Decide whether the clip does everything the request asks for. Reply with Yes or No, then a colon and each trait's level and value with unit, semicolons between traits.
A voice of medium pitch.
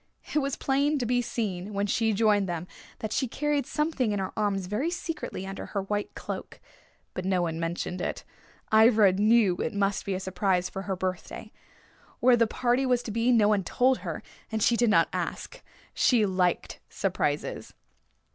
No: high, 210 Hz